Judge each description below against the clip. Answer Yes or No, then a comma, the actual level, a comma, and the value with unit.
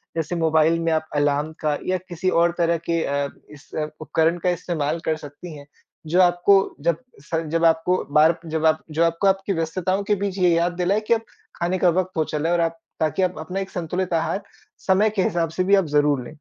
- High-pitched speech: No, medium, 165 Hz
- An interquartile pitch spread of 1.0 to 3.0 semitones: Yes, average, 2.7 semitones